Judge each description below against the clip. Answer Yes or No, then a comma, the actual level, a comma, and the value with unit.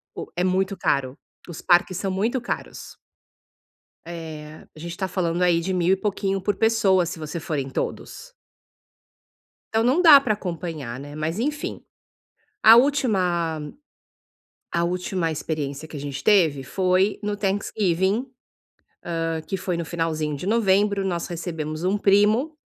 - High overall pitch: No, medium, 180 Hz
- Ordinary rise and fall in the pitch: Yes, average, 4.0 semitones